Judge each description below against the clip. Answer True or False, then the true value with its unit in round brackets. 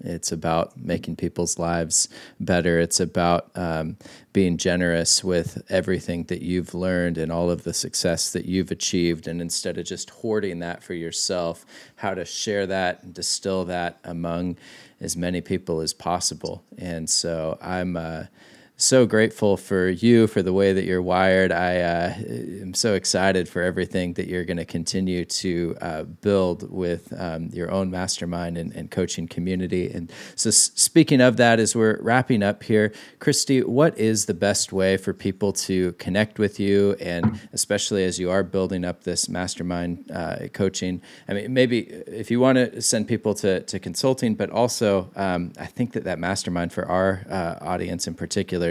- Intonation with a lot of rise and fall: False (2.7 semitones)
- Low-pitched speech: True (90 Hz)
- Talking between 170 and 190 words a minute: True (175 wpm)